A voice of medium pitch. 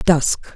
Yes: medium, 160 Hz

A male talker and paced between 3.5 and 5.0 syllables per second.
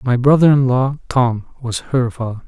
Yes: male; 4.7 syllables/s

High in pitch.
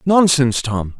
No: medium, 140 Hz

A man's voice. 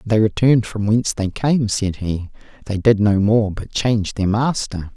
Yes: male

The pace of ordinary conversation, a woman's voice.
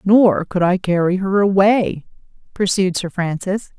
Yes: average, 145 wpm; female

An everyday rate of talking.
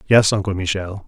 Yes: average, 165 wpm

